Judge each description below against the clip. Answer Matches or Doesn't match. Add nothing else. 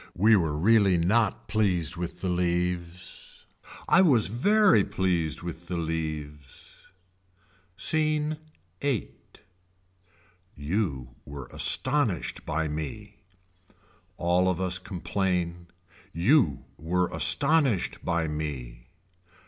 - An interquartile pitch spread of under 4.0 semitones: Doesn't match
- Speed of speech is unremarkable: Doesn't match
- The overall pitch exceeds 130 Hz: Doesn't match